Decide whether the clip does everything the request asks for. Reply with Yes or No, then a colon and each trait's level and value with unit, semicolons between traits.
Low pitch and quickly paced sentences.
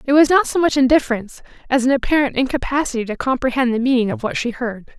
No: very high, 260 Hz; fast, 215 wpm